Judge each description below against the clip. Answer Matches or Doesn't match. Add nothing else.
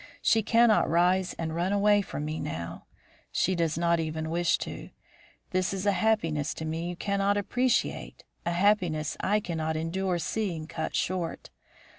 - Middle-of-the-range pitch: Matches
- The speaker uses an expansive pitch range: Doesn't match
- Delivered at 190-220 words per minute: Doesn't match